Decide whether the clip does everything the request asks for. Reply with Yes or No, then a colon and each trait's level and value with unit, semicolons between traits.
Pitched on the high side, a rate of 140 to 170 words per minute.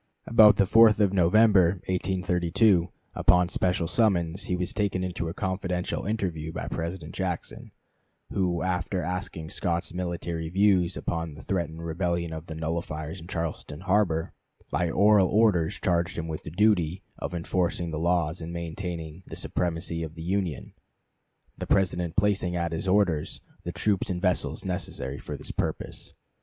No: very low, 90 Hz; average, 155 wpm